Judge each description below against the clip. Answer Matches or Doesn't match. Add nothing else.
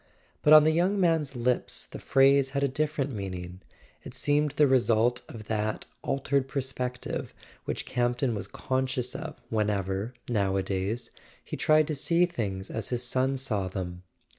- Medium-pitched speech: Doesn't match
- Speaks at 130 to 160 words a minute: Matches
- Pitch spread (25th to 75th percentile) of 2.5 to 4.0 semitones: Doesn't match